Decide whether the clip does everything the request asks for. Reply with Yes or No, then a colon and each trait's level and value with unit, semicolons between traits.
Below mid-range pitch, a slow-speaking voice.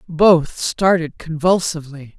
No: medium, 160 Hz; slow, 80 wpm